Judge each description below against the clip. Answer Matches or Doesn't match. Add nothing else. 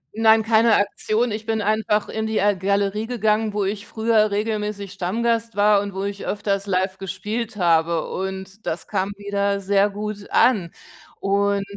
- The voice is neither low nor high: Doesn't match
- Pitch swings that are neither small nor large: Doesn't match